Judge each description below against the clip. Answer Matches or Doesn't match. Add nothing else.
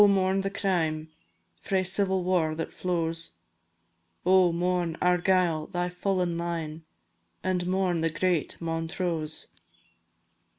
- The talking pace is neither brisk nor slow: Doesn't match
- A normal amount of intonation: Doesn't match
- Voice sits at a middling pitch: Matches